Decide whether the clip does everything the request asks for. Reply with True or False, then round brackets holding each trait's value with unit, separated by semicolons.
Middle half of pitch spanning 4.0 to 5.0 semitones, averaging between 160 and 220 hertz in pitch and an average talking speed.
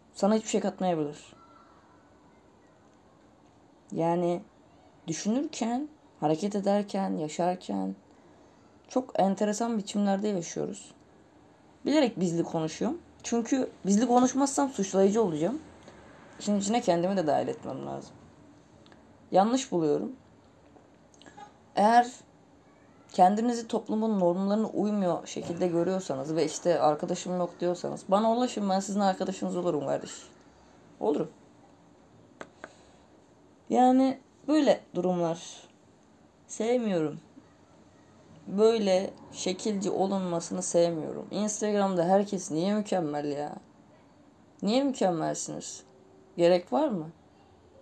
False (4.3 semitones; 190 Hz; 85 wpm)